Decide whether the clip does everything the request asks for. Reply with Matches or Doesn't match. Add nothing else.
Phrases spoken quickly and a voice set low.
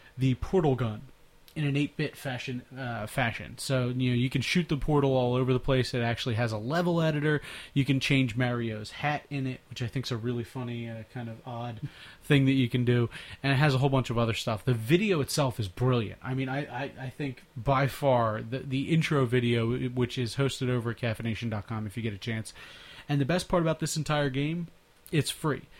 Matches